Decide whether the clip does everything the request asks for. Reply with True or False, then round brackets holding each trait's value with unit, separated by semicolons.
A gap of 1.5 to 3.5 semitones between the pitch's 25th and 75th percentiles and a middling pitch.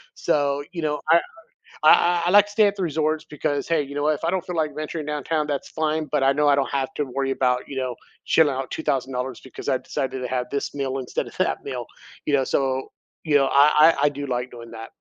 True (2.6 semitones; 145 Hz)